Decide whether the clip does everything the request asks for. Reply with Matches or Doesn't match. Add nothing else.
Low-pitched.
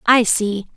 Doesn't match